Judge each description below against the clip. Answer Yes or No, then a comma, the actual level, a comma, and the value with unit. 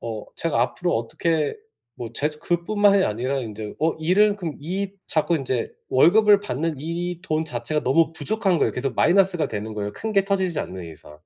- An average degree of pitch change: No, wide, 7.0 semitones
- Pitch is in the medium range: Yes, medium, 160 Hz